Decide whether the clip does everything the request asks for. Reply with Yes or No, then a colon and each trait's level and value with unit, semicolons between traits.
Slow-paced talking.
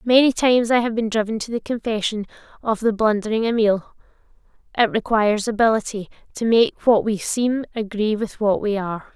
No: average, 170 wpm